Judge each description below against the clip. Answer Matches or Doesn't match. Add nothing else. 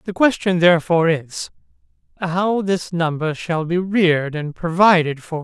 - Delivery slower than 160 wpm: Matches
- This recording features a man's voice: Matches